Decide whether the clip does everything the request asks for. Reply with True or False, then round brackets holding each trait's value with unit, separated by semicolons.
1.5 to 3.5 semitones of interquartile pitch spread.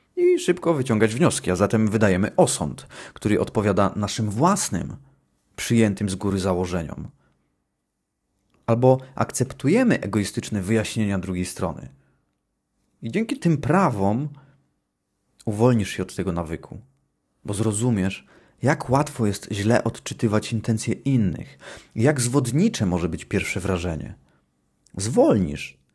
False (5.4 semitones)